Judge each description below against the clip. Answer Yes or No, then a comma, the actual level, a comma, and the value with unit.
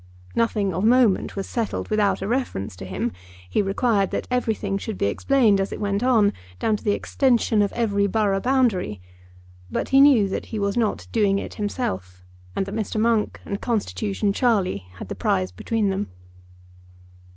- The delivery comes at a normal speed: Yes, average, 175 wpm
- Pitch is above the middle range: Yes, high, 205 Hz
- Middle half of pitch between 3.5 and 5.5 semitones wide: No, average, 2.8 semitones